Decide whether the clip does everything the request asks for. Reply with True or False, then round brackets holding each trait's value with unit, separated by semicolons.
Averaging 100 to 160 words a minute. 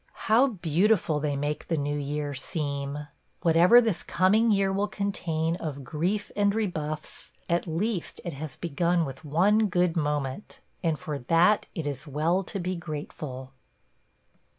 True (150 wpm)